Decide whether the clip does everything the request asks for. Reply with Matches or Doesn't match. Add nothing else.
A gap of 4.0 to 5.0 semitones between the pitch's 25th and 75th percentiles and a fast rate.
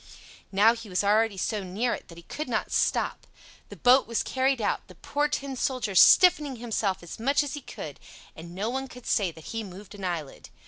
Doesn't match